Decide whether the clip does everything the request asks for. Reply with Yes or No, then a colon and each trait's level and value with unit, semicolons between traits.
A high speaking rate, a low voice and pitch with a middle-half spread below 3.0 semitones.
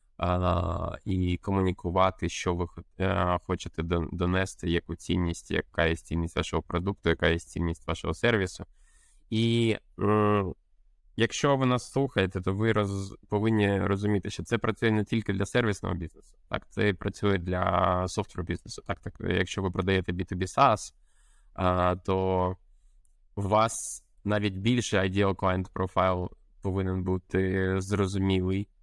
No: average, 135 wpm; very low, 95 Hz; narrow, 2.6 semitones